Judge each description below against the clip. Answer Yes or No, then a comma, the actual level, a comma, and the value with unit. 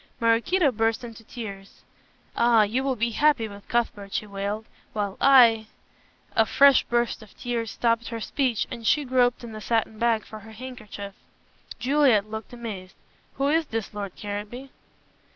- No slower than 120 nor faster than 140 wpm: No, average, 165 wpm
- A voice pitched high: Yes, high, 230 Hz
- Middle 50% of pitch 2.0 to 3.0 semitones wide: Yes, average, 2.7 semitones